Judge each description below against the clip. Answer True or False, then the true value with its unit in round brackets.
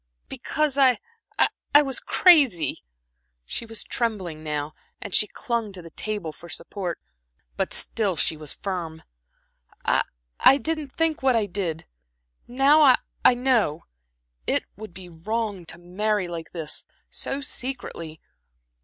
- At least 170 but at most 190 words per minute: False (135 wpm)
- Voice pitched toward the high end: True (205 Hz)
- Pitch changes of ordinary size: False (7.2 semitones)